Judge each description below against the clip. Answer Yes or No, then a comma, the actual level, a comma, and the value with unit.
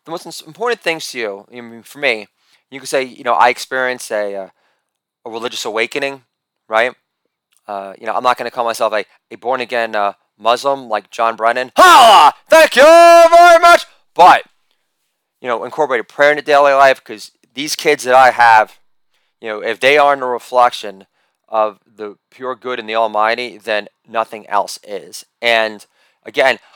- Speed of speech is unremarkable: Yes, average, 180 wpm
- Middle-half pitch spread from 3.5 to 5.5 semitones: Yes, average, 4.7 semitones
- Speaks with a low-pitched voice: Yes, low, 125 Hz